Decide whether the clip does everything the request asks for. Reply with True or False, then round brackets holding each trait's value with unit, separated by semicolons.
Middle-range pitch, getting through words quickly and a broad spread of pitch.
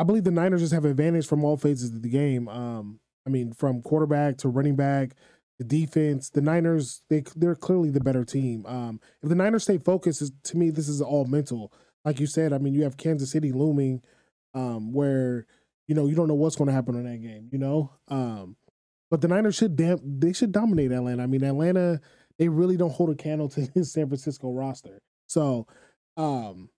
False (145 Hz; 210 wpm; 3.8 semitones)